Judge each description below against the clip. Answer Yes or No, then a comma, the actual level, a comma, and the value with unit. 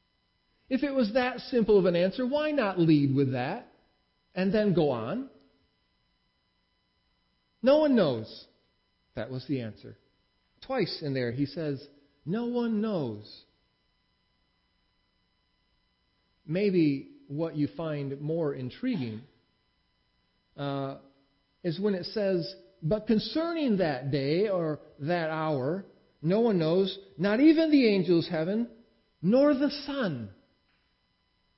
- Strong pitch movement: Yes, wide, 8.0 semitones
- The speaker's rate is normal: No, slow, 115 wpm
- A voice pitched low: No, medium, 165 Hz